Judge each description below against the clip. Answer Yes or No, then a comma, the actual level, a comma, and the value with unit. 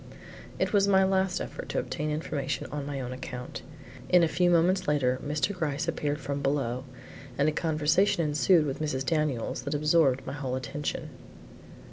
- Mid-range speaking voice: Yes, medium, 150 Hz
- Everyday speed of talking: Yes, average, 170 wpm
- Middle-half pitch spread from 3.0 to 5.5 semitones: Yes, average, 3.5 semitones